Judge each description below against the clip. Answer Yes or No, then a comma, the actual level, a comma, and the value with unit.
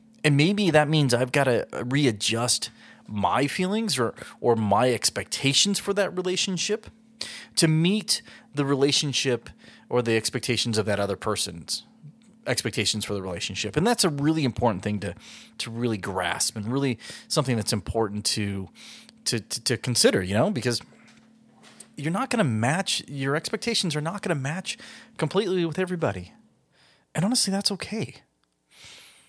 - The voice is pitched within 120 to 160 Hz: Yes, medium, 140 Hz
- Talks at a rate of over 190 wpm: No, average, 150 wpm